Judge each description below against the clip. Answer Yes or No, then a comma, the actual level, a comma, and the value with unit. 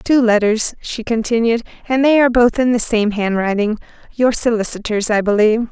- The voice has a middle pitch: No, high, 225 Hz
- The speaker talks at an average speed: Yes, average, 160 wpm